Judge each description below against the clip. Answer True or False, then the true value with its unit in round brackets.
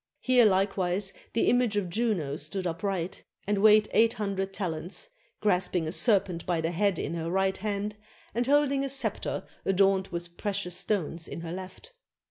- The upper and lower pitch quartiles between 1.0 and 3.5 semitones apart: True (3.2 semitones)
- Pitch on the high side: True (195 Hz)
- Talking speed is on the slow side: False (170 wpm)